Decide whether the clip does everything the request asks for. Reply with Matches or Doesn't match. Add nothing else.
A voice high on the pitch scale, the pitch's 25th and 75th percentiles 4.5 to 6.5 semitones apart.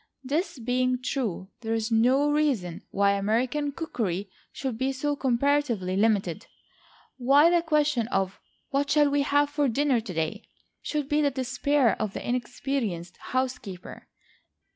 Matches